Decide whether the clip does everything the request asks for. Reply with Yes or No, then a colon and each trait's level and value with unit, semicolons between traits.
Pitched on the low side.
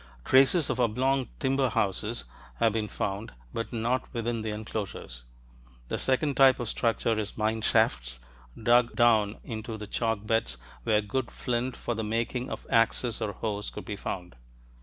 Yes: low, 115 Hz